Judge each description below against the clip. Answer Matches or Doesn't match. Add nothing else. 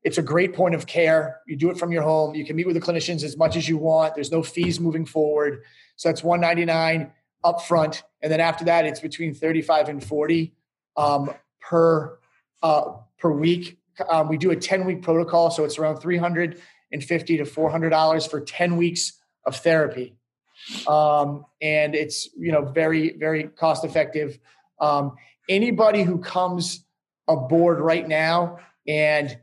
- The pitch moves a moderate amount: Doesn't match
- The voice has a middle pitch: Matches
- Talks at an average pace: Matches